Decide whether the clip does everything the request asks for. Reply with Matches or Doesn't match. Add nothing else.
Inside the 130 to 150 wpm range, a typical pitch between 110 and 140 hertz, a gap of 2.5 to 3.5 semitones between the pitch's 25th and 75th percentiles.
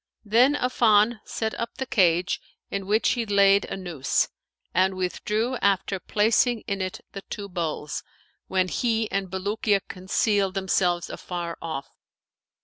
Doesn't match